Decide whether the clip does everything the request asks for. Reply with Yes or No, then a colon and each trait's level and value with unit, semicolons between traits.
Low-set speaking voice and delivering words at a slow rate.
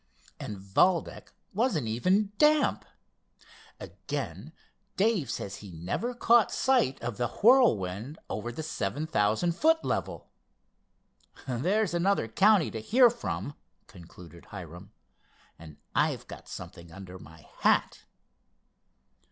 Yes: low, 130 Hz; slow, 110 wpm